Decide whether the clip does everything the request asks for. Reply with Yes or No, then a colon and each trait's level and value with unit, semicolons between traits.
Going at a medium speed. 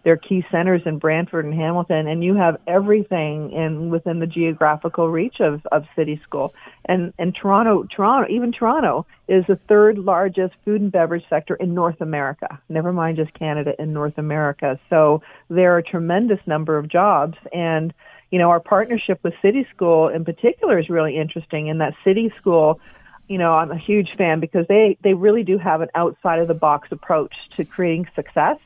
Yes: average, 190 wpm